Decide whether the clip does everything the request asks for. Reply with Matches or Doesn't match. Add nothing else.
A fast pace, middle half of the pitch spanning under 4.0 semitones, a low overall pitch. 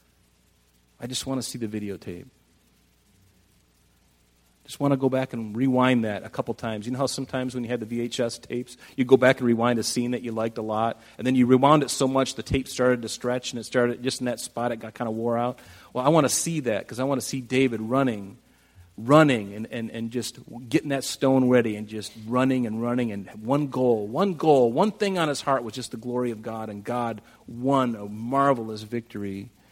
Matches